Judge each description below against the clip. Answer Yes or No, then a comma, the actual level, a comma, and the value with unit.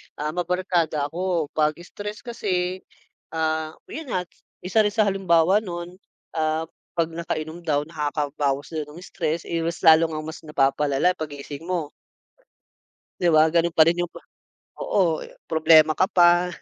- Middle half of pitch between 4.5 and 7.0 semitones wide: No, narrow, 2.5 semitones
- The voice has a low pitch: No, medium, 165 Hz